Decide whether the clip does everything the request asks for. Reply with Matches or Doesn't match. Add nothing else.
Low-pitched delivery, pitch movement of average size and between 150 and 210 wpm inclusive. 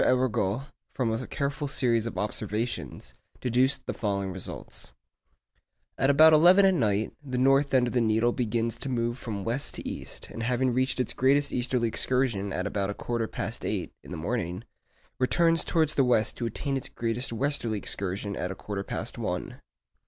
Matches